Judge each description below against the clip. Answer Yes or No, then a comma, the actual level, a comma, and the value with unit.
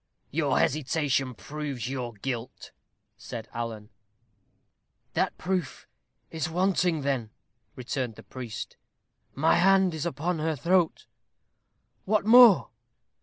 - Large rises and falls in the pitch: Yes, wide, 5.7 semitones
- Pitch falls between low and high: Yes, medium, 150 Hz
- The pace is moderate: No, slow, 105 wpm